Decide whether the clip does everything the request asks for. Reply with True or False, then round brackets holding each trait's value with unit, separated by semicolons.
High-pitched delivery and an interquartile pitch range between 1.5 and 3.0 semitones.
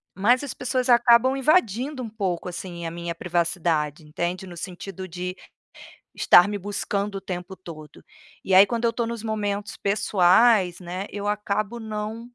False (200 Hz; 4.4 semitones)